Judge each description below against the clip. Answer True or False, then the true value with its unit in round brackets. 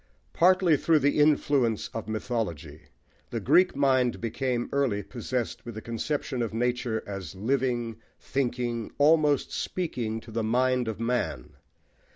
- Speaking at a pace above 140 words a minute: False (135 wpm)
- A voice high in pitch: False (120 Hz)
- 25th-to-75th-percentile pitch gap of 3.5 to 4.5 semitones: True (3.8 semitones)